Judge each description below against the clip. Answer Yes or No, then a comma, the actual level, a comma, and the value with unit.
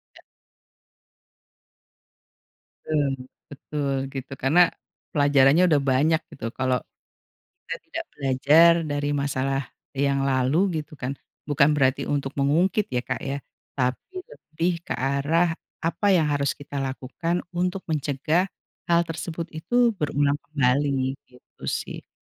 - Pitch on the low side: No, medium, 145 Hz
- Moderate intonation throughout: Yes, average, 3.0 semitones